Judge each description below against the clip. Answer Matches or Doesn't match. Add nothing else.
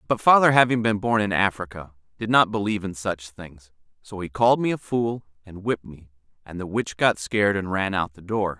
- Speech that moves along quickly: Matches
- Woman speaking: Doesn't match